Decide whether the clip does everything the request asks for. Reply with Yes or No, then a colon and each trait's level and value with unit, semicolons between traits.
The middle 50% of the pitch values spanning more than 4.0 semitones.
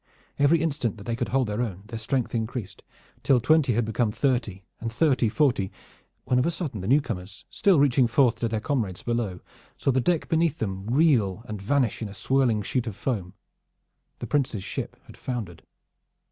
Yes: average, 4.5 semitones